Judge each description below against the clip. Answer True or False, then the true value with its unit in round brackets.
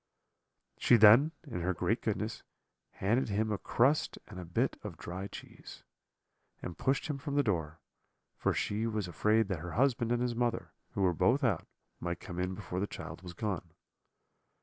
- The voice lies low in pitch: True (105 Hz)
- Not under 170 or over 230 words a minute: True (180 wpm)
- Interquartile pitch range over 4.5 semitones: True (5.2 semitones)